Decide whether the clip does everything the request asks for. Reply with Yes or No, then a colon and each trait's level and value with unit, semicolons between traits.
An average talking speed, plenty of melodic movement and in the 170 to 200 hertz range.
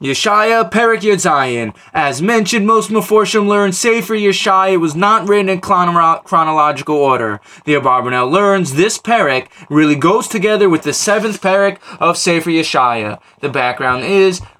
Yes: average, 145 wpm; wide, 6.4 semitones; medium, 185 Hz